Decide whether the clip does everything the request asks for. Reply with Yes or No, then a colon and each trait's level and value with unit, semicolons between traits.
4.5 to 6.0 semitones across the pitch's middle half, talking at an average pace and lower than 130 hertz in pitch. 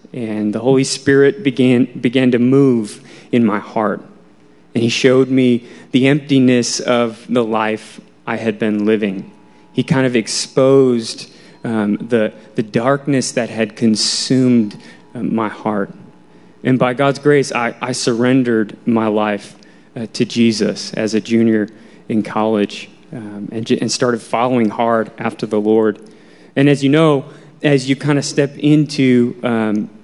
No: average, 3.3 semitones; average, 150 wpm; low, 120 Hz